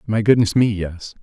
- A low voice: Yes, low, 105 Hz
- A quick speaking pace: No, average, 195 wpm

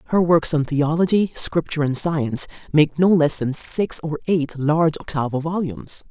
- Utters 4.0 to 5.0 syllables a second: No, 5.2 syllables/s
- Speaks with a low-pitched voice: No, medium, 155 Hz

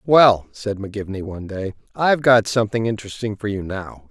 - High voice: No, low, 105 Hz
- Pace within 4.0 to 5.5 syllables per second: No, 5.9 syllables/s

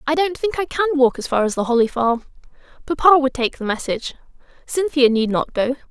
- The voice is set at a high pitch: Yes, very high, 270 Hz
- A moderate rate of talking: No, fast, 215 wpm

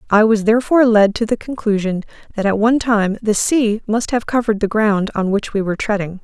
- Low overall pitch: No, high, 215 Hz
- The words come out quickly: Yes, fast, 220 wpm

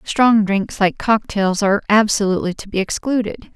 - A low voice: No, high, 205 Hz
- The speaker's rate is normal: Yes, average, 150 wpm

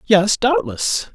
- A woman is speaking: No, male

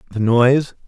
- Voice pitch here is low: Yes, low, 125 Hz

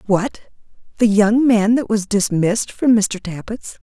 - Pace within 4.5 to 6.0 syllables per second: No, 4.3 syllables/s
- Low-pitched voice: No, high, 215 Hz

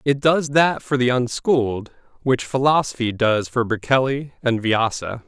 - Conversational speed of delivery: Yes, average, 150 wpm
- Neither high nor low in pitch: No, low, 125 Hz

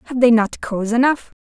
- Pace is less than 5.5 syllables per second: No, 6.3 syllables/s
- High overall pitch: Yes, high, 235 Hz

